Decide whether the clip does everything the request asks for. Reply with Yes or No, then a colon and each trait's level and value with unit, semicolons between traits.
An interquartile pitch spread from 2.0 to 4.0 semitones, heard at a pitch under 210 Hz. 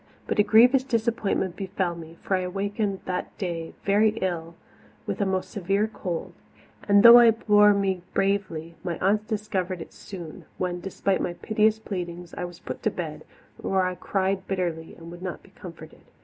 Yes: average, 2.9 semitones; high, 190 Hz